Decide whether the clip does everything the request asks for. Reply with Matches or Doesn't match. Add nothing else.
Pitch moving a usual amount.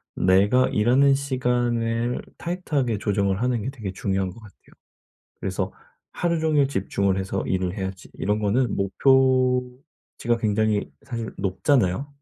Matches